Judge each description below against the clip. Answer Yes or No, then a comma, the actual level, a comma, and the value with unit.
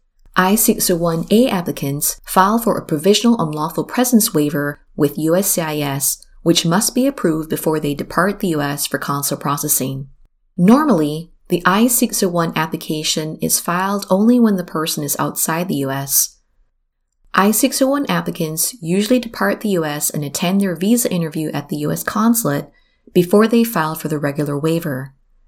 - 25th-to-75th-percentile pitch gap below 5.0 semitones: No, wide, 5.4 semitones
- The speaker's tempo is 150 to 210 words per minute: No, average, 140 wpm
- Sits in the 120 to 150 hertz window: No, medium, 165 Hz